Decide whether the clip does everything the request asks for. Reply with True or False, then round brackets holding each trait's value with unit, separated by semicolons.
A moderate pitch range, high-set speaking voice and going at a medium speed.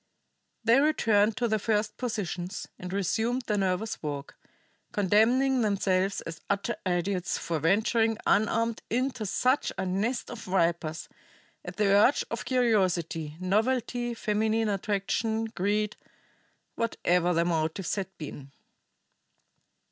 False (3.8 semitones; 205 Hz; 120 wpm)